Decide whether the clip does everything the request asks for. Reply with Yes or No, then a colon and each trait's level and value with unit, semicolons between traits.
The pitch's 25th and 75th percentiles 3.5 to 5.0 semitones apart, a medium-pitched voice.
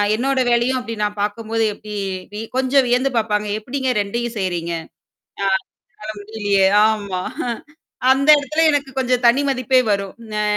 No: average, 3.9 semitones; high, 230 Hz